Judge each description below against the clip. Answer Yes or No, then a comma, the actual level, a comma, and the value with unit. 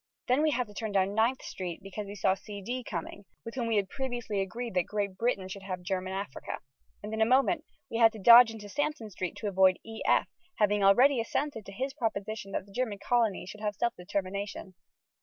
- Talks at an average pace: No, fast, 215 wpm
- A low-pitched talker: No, high, 210 Hz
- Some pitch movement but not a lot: Yes, average, 3.4 semitones